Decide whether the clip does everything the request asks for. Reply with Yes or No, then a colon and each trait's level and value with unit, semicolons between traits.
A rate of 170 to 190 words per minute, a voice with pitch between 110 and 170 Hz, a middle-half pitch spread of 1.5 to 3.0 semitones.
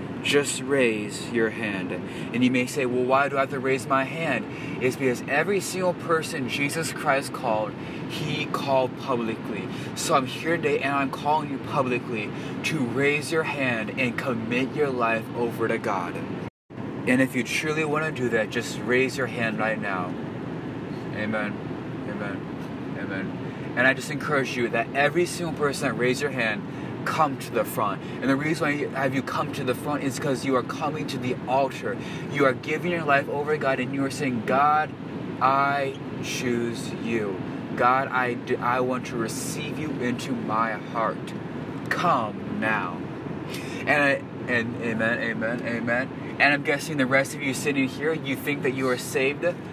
Yes: average, 180 wpm; low, 135 Hz; average, 2.7 semitones